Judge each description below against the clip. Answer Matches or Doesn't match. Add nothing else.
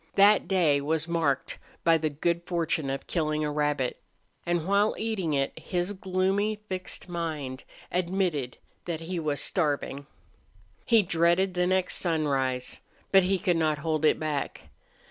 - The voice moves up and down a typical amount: Matches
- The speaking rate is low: Doesn't match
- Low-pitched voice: Doesn't match